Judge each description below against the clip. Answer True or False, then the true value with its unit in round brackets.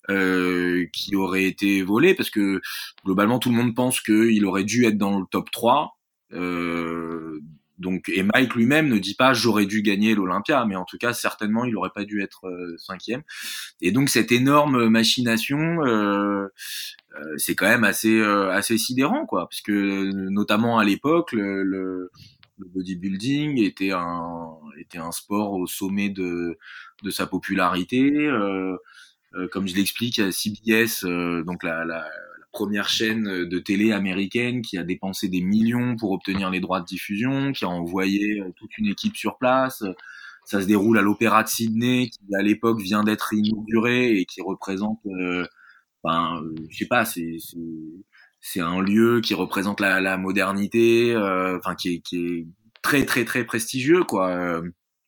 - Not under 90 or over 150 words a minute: False (170 wpm)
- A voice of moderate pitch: False (100 Hz)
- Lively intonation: False (3.7 semitones)